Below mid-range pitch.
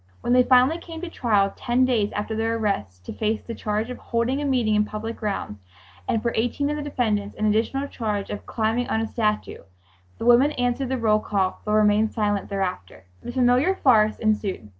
No: high, 225 Hz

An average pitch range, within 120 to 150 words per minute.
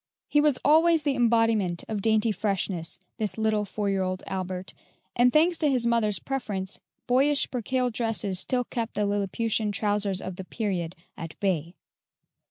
No: average, 4.3 semitones; average, 160 wpm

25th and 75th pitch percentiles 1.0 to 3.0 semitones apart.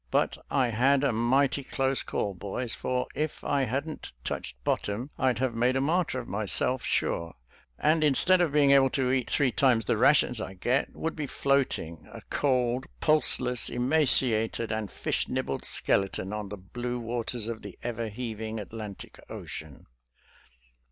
No: average, 3.9 semitones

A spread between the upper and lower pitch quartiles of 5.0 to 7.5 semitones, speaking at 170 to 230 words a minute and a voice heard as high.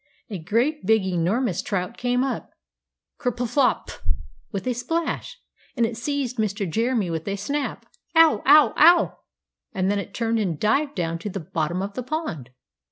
Yes: wide, 5.4 semitones; average, 180 wpm; high, 225 Hz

